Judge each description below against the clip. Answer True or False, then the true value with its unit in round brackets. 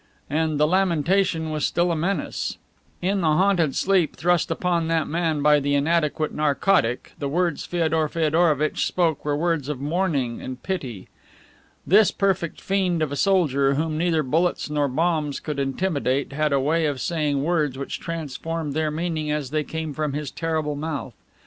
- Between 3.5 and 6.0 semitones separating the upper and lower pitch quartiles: False (2.8 semitones)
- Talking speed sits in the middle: True (170 wpm)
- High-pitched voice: False (155 Hz)